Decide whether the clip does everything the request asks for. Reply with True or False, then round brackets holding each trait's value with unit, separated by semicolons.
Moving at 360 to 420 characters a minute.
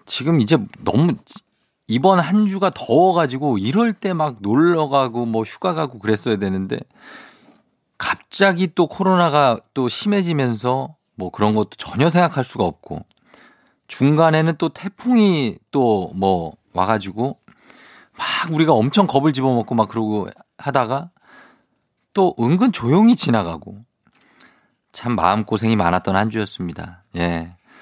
False (265 characters per minute)